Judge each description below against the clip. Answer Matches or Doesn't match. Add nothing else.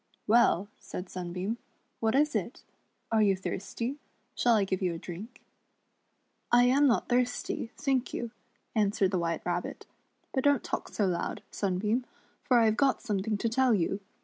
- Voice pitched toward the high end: Matches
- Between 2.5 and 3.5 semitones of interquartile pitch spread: Doesn't match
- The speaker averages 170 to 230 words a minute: Matches